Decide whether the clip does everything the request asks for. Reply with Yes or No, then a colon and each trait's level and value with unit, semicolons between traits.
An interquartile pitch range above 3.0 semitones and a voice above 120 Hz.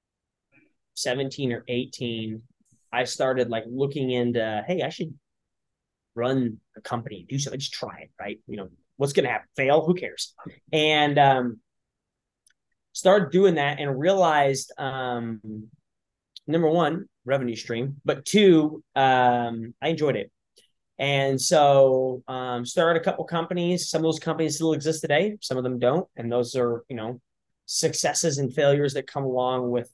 Yes: average, 4.3 semitones; low, 135 Hz